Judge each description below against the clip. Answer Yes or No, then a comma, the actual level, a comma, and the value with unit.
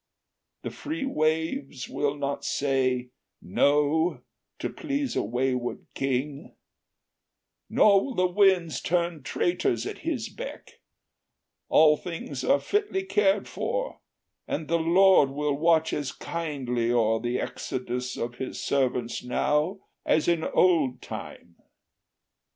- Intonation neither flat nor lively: No, wide, 5.7 semitones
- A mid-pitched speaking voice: Yes, medium, 150 Hz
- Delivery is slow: Yes, slow, 120 wpm